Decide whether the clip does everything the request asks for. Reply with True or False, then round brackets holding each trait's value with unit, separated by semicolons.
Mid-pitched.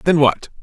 True (150 Hz)